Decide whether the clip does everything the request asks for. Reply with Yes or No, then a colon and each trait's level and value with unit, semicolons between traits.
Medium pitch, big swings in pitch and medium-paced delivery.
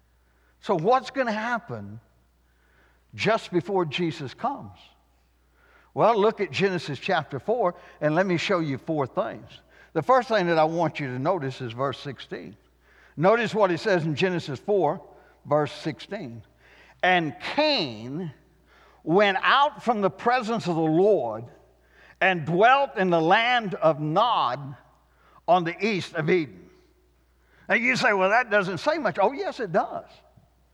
Yes: medium, 170 Hz; wide, 7.2 semitones; average, 150 wpm